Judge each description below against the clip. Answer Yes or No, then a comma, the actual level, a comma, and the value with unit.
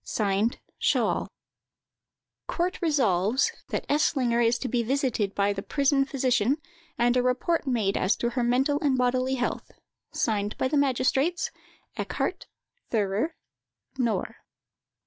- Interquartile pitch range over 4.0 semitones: No, average, 3.6 semitones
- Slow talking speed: Yes, slow, 125 wpm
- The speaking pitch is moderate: No, very high, 250 Hz